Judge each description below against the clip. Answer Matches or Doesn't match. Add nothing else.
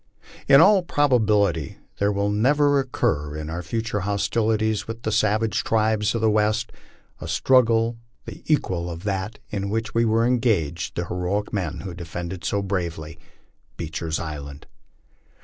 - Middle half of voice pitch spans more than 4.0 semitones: Matches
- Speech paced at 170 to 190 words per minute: Doesn't match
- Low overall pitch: Matches